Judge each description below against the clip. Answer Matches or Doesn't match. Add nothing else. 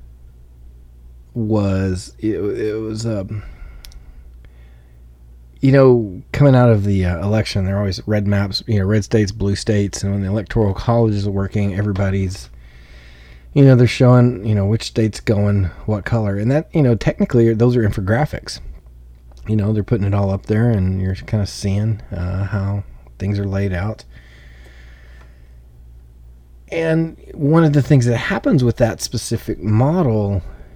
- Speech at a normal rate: Matches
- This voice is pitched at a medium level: Doesn't match